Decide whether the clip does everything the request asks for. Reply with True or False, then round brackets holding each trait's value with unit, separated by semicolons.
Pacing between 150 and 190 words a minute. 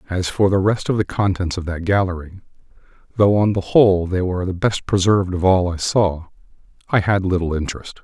False (200 wpm)